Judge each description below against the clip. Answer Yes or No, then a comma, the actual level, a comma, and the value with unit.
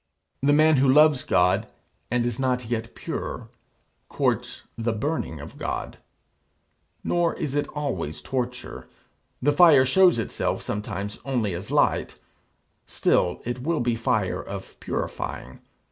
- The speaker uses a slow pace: Yes, slow, 130 wpm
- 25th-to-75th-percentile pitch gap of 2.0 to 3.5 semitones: No, average, 4.7 semitones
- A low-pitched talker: Yes, low, 125 Hz